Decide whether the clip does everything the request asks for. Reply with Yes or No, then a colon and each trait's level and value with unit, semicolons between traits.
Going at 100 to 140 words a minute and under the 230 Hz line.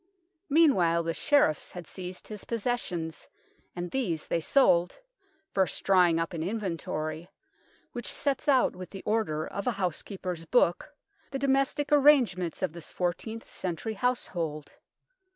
Yes: slow, 135 wpm; medium, 185 Hz